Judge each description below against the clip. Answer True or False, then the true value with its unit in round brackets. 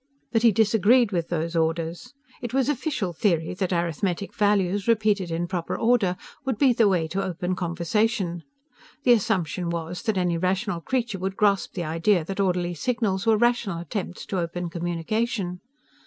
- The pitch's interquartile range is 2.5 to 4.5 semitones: True (4.2 semitones)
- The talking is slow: False (165 wpm)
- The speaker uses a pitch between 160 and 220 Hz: True (190 Hz)